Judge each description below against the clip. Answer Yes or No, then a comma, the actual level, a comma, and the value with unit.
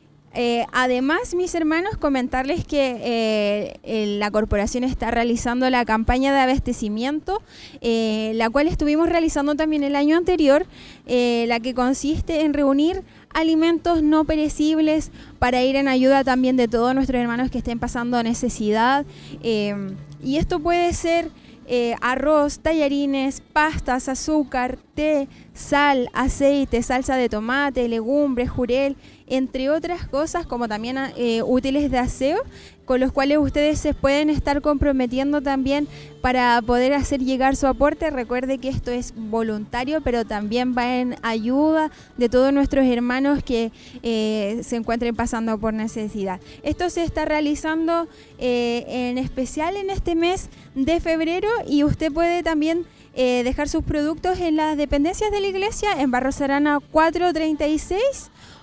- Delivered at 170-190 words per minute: No, average, 145 wpm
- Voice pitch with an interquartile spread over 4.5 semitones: No, average, 4.0 semitones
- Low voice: No, very high, 270 Hz